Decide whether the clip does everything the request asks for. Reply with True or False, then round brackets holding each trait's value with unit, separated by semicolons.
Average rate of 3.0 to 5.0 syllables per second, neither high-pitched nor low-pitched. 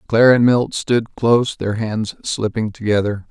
False (4.6 syllables/s; 110 Hz)